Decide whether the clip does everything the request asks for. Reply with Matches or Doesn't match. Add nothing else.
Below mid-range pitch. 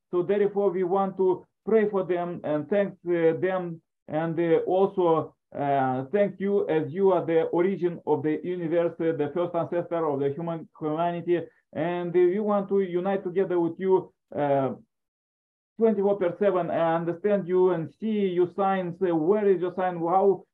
Doesn't match